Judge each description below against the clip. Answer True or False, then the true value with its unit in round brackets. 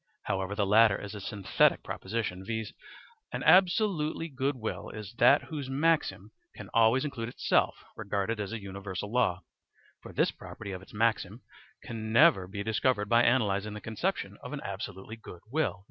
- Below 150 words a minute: False (165 wpm)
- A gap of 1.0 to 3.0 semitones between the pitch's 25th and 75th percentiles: False (4.3 semitones)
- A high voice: False (110 Hz)